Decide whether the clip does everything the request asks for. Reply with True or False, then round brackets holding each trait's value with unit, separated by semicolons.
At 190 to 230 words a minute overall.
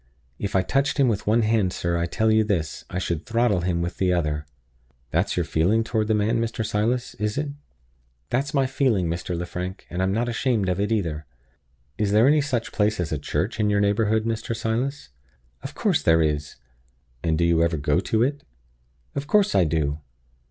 True (200 wpm)